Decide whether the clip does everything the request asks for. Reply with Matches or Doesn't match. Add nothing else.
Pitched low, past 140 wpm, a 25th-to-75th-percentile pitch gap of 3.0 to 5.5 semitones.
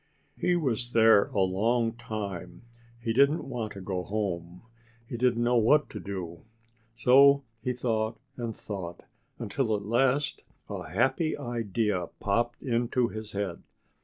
Doesn't match